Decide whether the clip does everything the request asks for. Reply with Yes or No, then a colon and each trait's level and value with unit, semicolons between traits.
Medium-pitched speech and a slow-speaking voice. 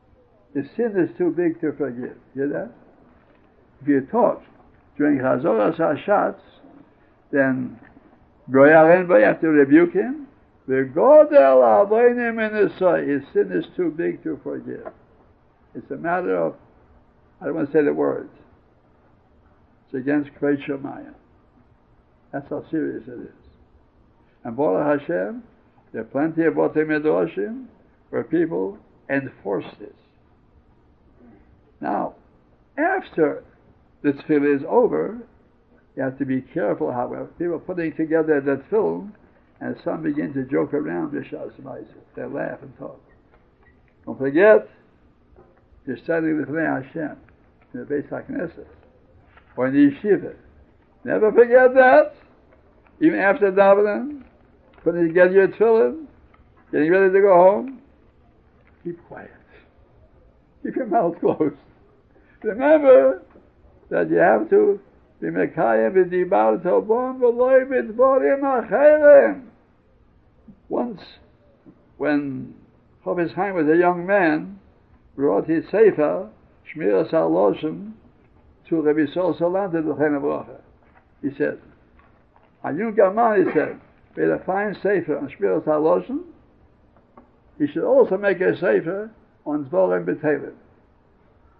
Yes: medium, 170 Hz; slow, 120 wpm